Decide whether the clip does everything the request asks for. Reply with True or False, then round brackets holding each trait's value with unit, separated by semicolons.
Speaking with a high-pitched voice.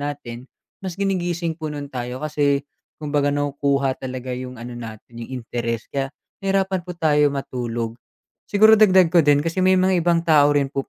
False (145 Hz)